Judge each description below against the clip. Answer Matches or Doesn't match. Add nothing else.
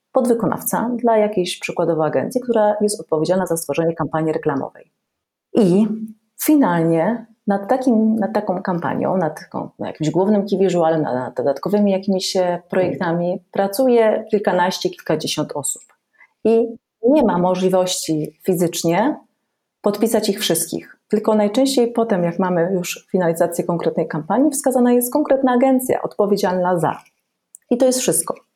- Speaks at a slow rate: Doesn't match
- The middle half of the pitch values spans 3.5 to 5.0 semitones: Matches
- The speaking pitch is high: Matches